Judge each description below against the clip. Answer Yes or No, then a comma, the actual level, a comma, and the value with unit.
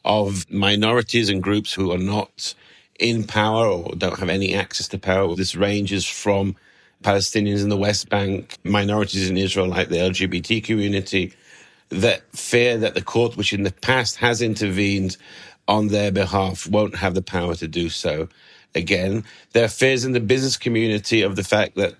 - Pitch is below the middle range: Yes, low, 100 Hz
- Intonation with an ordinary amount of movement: No, narrow, 2.3 semitones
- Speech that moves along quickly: No, average, 175 wpm